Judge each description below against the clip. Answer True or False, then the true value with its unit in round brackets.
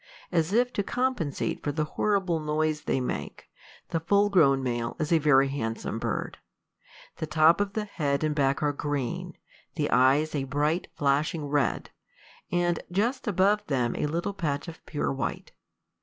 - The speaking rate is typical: True (165 wpm)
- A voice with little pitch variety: False (4.2 semitones)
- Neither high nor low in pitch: True (155 Hz)